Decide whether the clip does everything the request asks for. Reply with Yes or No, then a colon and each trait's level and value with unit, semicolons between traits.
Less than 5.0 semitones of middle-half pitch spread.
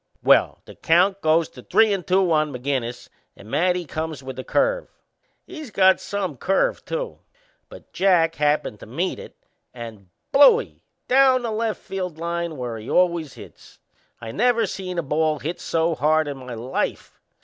No: wide, 5.5 semitones